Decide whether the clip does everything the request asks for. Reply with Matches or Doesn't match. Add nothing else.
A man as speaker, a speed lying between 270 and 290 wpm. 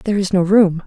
Doesn't match